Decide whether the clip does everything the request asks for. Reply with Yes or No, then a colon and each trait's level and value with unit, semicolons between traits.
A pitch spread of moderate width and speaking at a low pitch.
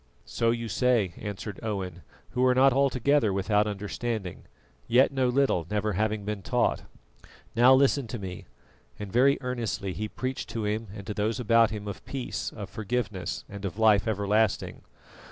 Yes: average, 3.4 semitones; low, 110 Hz